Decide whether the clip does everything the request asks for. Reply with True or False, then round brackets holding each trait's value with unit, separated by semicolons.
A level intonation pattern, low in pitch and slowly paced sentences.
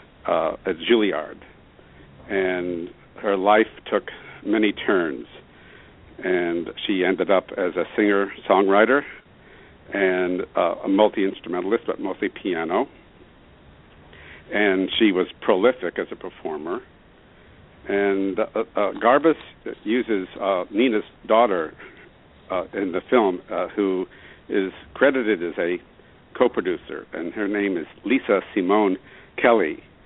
True (2.2 semitones; 95 Hz; 110 wpm)